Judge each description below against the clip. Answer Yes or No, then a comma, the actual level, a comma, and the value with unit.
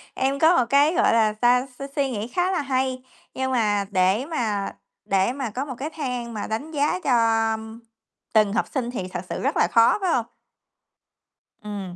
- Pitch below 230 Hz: No, very high, 250 Hz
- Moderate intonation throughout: Yes, average, 4.8 semitones